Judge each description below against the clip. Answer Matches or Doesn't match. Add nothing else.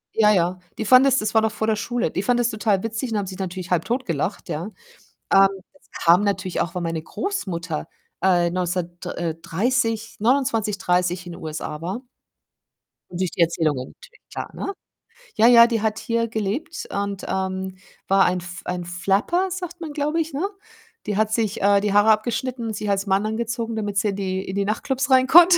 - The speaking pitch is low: Doesn't match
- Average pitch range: Matches